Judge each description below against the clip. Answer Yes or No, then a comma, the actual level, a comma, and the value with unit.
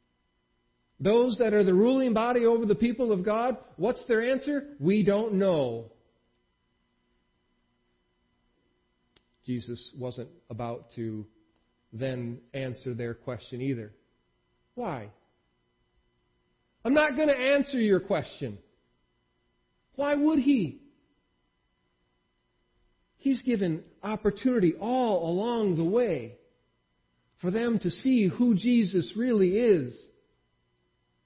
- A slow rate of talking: Yes, slow, 100 wpm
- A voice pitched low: No, medium, 145 Hz